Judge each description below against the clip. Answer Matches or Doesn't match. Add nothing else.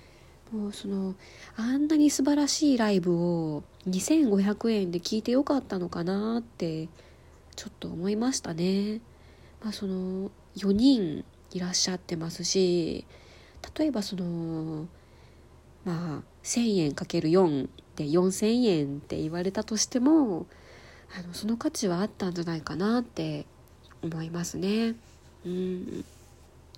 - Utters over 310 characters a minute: Doesn't match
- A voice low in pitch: Doesn't match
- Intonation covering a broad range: Doesn't match